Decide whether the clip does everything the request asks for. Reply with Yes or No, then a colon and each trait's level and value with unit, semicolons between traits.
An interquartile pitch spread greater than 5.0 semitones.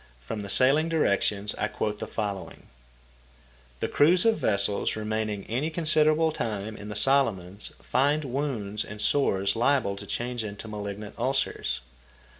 Yes: wide, 5.5 semitones